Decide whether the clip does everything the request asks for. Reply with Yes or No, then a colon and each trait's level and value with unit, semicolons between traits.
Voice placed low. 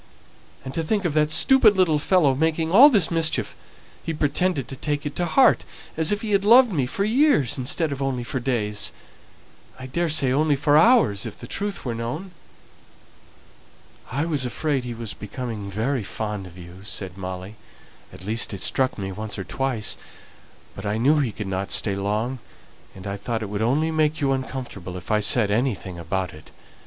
Yes: low, 130 Hz